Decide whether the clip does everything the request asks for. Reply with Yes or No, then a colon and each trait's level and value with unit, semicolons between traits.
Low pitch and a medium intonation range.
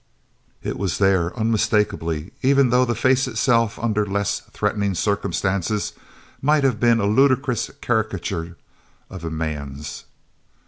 Yes: low, 105 Hz; average, 4.5 semitones